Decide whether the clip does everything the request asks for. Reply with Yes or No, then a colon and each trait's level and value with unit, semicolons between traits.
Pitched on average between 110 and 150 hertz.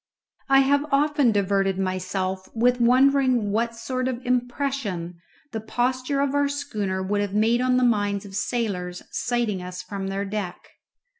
No: high, 230 Hz